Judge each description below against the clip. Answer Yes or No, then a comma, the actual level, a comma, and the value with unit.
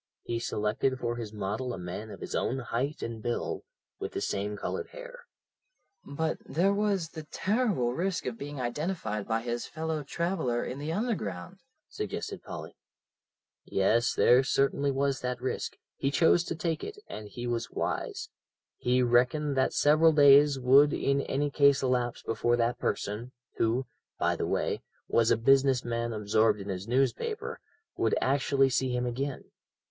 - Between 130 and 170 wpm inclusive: Yes, average, 160 wpm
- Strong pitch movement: No, average, 4.1 semitones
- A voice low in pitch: Yes, low, 130 Hz